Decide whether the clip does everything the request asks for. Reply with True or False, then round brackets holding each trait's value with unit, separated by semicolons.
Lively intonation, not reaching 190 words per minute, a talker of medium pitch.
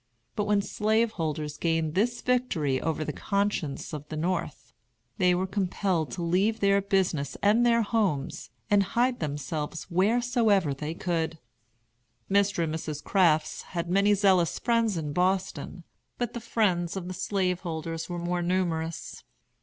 False (4.0 semitones; 145 wpm; 180 Hz)